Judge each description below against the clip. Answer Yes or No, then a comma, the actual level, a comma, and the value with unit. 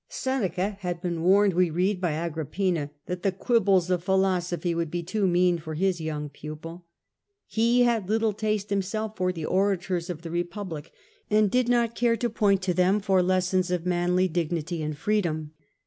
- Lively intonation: No, average, 3.0 semitones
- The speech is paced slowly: No, average, 180 wpm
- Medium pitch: Yes, medium, 180 Hz